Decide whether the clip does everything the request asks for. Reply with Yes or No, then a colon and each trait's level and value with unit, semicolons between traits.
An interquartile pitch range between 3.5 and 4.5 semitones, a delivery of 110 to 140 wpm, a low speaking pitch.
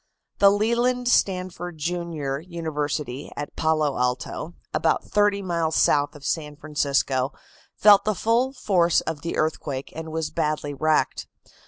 No: average, 4.0 semitones; slow, 135 wpm; medium, 160 Hz